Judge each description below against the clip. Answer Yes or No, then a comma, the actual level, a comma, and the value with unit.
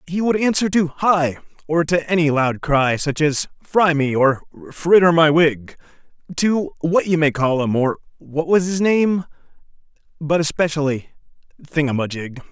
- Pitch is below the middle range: No, medium, 160 Hz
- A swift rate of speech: No, average, 170 wpm